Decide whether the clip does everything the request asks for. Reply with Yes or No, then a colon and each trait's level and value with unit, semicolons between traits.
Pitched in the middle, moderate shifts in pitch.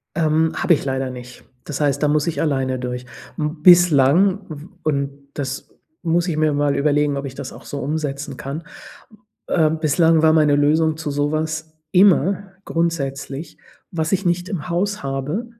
Yes: medium, 155 Hz; average, 3.0 semitones